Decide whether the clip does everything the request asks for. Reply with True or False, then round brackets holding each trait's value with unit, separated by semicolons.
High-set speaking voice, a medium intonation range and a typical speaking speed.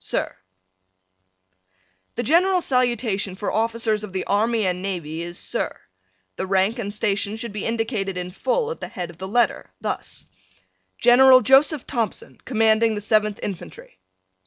True (215 Hz; 3.8 semitones; 150 wpm)